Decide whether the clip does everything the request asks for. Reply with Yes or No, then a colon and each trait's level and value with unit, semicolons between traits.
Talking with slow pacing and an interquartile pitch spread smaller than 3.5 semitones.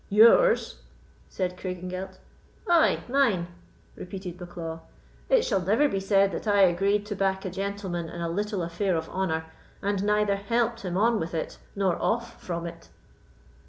No: average, 160 wpm; average, 2.9 semitones